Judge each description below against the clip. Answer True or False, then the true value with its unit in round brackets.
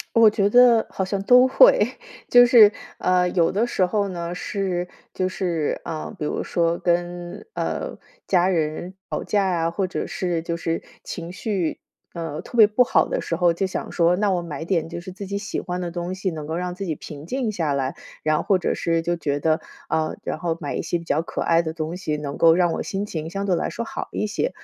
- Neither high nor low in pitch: True (175 Hz)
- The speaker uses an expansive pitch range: False (3.1 semitones)